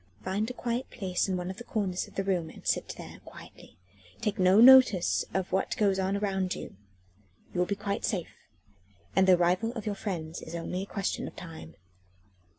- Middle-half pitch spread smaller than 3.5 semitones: Yes, narrow, 2.5 semitones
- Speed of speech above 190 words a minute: Yes, average, 200 wpm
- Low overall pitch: No, high, 190 Hz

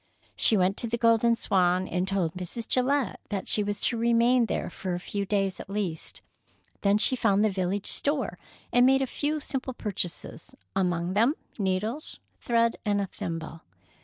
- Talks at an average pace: Yes, average, 175 wpm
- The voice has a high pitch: Yes, high, 205 Hz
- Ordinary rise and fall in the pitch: Yes, average, 4.2 semitones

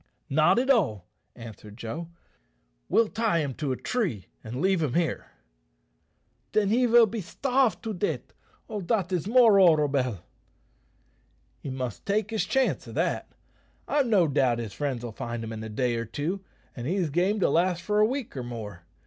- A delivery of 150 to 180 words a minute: Yes, average, 175 wpm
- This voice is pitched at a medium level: Yes, medium, 165 Hz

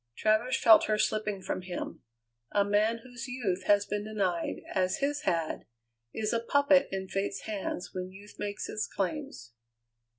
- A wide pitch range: No, average, 3.4 semitones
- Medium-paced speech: Yes, average, 160 wpm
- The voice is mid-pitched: No, high, 205 Hz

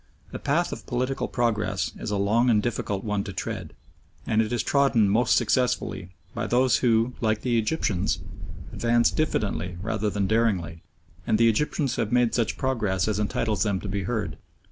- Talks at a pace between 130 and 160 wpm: No, average, 175 wpm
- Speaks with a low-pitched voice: Yes, low, 110 Hz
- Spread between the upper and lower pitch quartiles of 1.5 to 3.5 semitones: Yes, average, 3.1 semitones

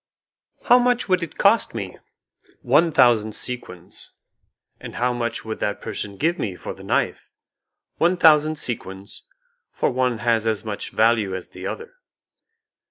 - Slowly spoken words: No, average, 150 wpm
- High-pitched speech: No, low, 120 Hz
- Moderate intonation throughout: No, wide, 7.0 semitones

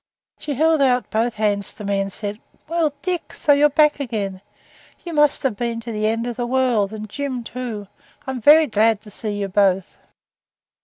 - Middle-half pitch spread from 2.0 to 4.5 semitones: No, average, 5.1 semitones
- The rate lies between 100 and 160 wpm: No, average, 195 wpm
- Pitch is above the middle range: Yes, high, 235 Hz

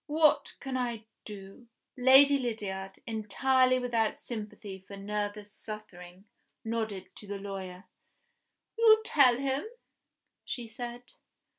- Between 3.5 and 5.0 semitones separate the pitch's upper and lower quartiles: Yes, average, 4.1 semitones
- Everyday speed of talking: No, slow, 110 wpm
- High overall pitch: Yes, high, 225 Hz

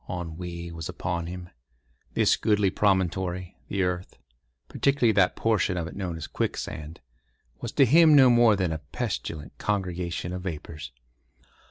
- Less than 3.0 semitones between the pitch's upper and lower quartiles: No, average, 3.5 semitones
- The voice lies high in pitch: No, very low, 90 Hz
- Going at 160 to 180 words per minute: No, slow, 135 wpm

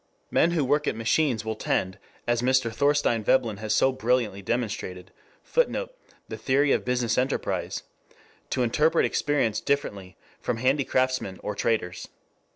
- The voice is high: No, low, 125 Hz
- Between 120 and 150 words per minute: Yes, average, 140 wpm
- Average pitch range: Yes, average, 4.3 semitones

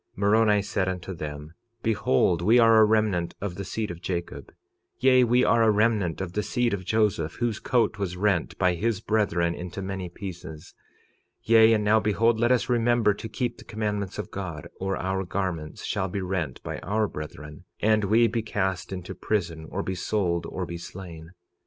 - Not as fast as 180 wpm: No, average, 190 wpm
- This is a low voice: Yes, low, 100 Hz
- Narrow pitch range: No, average, 3.8 semitones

